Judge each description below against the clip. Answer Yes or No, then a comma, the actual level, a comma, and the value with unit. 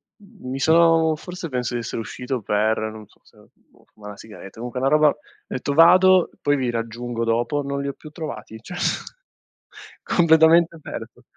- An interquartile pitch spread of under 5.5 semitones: No, wide, 5.8 semitones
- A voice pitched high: No, medium, 140 Hz